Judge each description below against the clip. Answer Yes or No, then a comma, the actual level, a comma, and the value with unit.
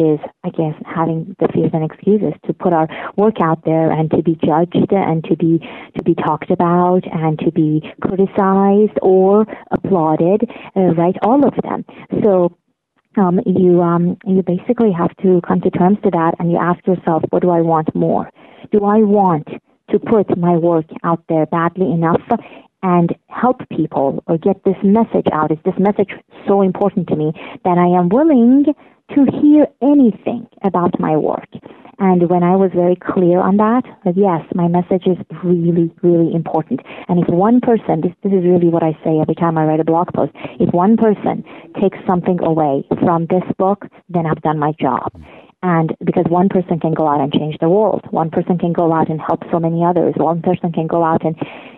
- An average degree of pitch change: Yes, average, 3.1 semitones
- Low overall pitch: No, medium, 180 Hz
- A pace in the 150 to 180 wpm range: No, average, 195 wpm